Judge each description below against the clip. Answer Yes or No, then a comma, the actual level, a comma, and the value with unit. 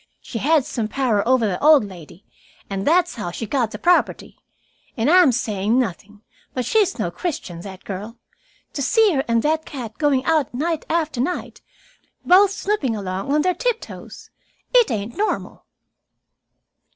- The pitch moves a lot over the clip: Yes, wide, 7.5 semitones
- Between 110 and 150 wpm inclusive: No, average, 165 wpm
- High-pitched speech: Yes, very high, 260 Hz